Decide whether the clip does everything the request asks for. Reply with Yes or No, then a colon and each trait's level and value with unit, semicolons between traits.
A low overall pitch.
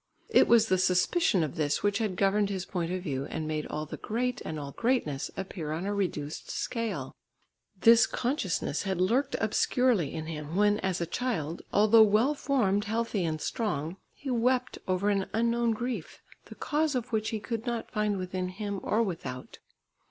No: high, 200 Hz